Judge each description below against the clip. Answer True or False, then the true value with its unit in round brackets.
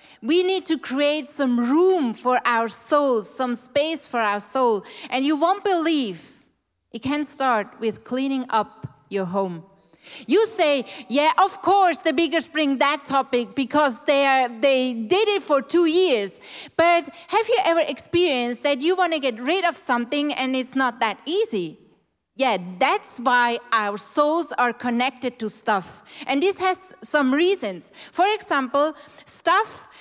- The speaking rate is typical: True (160 wpm)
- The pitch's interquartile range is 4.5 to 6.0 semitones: True (5.1 semitones)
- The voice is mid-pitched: False (280 Hz)